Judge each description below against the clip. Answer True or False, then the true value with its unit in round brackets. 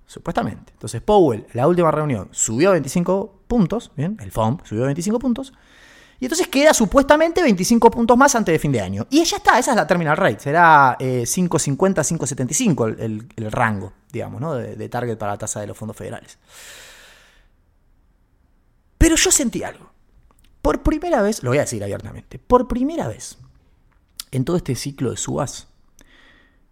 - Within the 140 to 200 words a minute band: True (170 wpm)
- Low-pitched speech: False (150 Hz)